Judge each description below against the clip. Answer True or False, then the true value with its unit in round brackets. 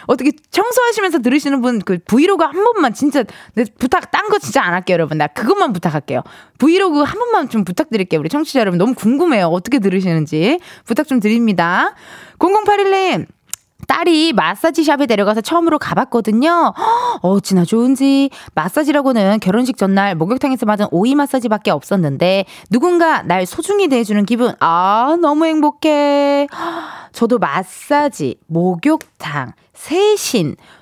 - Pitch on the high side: True (265 Hz)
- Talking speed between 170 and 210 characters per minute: False (340 characters per minute)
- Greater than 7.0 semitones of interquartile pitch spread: True (8.5 semitones)